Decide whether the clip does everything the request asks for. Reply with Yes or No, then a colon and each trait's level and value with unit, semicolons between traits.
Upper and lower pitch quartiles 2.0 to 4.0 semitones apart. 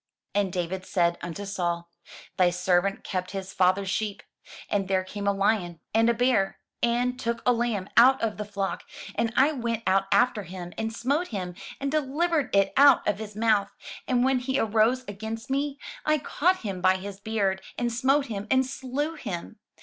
No: average, 4.7 semitones